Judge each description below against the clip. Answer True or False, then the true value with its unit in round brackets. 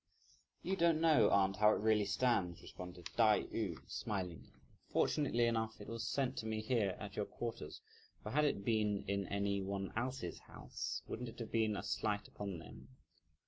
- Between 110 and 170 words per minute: False (180 wpm)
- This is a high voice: False (105 Hz)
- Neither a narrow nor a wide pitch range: True (3.0 semitones)